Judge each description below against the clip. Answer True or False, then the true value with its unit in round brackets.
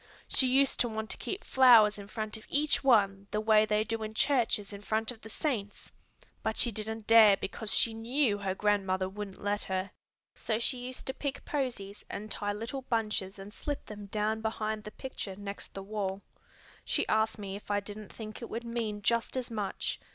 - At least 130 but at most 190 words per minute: False (205 wpm)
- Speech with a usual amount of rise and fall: False (2.3 semitones)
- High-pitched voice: True (215 Hz)